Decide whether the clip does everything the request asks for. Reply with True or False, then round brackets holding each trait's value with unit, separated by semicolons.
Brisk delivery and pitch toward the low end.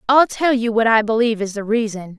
False (245 wpm; 225 Hz)